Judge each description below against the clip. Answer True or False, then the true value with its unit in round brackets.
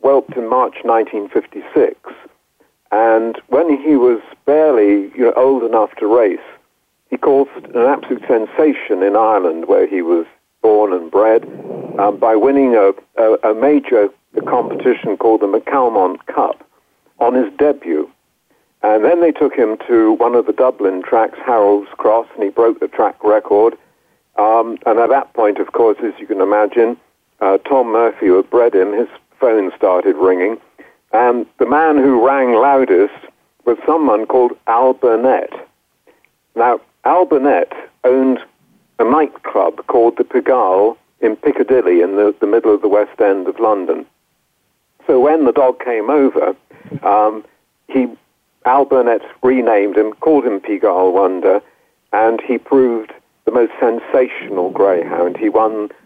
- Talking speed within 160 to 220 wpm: False (150 wpm)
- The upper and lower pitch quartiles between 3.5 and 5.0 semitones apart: False (5.5 semitones)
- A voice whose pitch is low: True (120 Hz)